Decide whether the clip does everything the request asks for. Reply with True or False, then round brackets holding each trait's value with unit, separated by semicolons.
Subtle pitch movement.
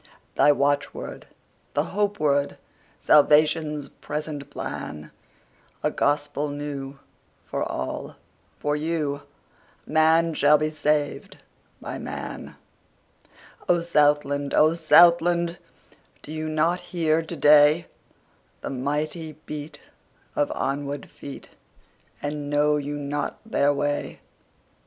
True (1.6 semitones)